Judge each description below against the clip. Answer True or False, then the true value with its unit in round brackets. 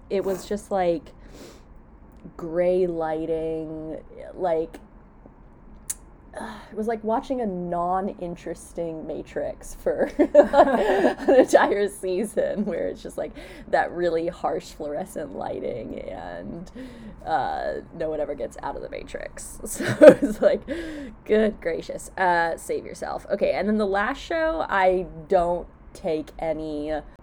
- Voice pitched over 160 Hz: True (185 Hz)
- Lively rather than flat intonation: True (6.3 semitones)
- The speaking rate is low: True (125 wpm)